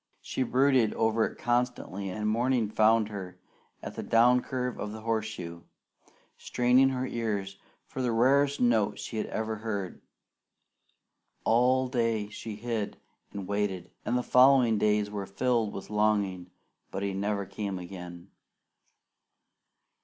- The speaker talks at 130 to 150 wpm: Yes, average, 140 wpm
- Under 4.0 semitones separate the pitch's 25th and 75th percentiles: Yes, average, 3.4 semitones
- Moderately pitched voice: No, low, 110 Hz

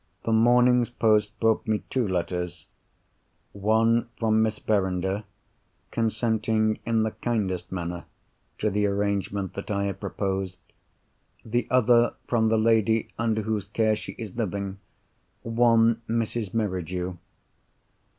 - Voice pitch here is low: Yes, low, 110 Hz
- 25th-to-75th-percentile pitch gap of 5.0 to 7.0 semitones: No, narrow, 2.5 semitones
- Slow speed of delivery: Yes, slow, 120 wpm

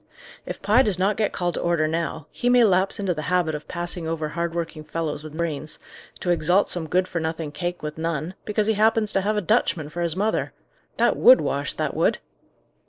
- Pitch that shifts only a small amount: No, average, 3.8 semitones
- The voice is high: No, medium, 175 Hz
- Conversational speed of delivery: No, fast, 220 wpm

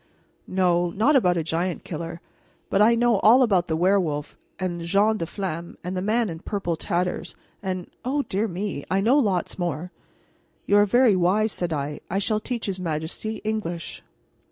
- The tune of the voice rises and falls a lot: No, average, 3.9 semitones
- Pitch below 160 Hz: No, medium, 185 Hz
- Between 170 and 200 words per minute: Yes, average, 180 wpm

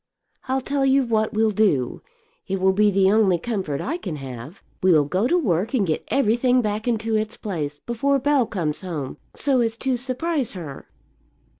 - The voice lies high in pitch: Yes, high, 215 Hz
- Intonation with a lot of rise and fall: Yes, wide, 5.7 semitones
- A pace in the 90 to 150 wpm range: No, average, 180 wpm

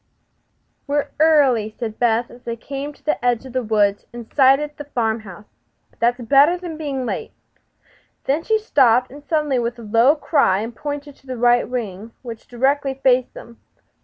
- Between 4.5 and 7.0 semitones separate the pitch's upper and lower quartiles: No, average, 3.7 semitones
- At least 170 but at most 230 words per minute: Yes, average, 185 wpm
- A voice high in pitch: Yes, very high, 250 Hz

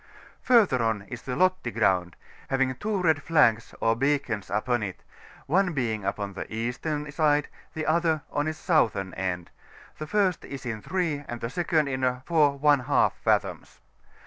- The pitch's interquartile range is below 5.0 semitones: No, wide, 5.6 semitones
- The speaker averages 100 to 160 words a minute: Yes, average, 155 wpm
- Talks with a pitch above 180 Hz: No, low, 135 Hz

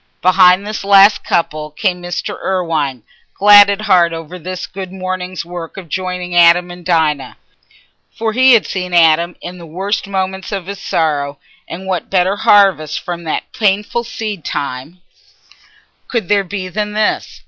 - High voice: No, medium, 180 Hz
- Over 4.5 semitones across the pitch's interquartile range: No, average, 2.7 semitones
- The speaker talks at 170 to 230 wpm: No, average, 160 wpm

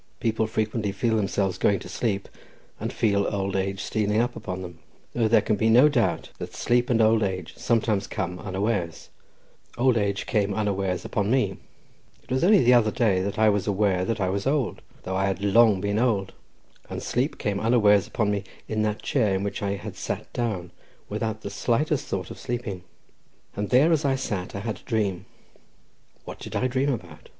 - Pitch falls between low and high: No, low, 105 Hz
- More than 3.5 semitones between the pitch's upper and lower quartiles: No, average, 3.2 semitones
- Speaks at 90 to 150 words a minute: No, average, 190 wpm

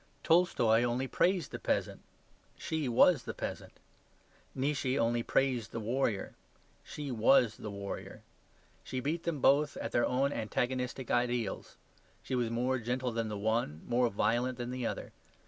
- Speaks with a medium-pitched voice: No, low, 125 Hz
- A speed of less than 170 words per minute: Yes, average, 150 wpm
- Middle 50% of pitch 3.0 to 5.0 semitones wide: No, narrow, 2.6 semitones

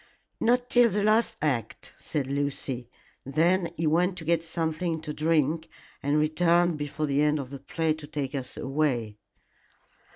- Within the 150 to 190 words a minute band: Yes, average, 160 wpm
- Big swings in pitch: No, average, 3.1 semitones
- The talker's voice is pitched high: No, medium, 155 Hz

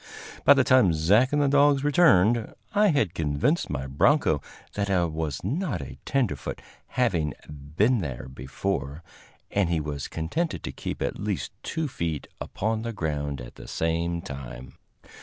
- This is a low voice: Yes, very low, 90 Hz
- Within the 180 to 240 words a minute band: No, average, 160 wpm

